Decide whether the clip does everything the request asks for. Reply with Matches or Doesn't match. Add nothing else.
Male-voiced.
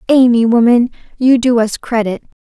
Doesn't match